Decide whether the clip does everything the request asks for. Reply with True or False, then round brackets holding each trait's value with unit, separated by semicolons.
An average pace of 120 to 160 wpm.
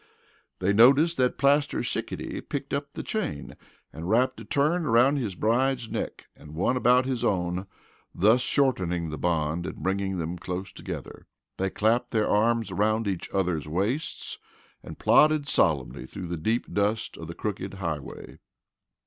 True (155 wpm)